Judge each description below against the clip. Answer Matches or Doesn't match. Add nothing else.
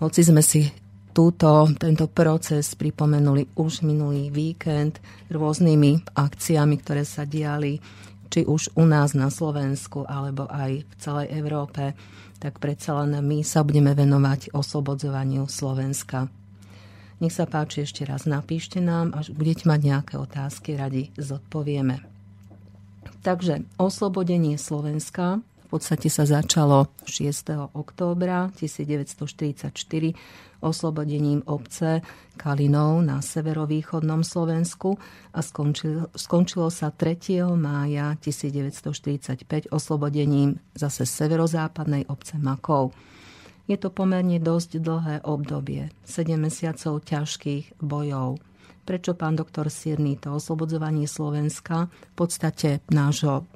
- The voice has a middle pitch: Matches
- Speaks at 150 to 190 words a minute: Doesn't match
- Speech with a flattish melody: Matches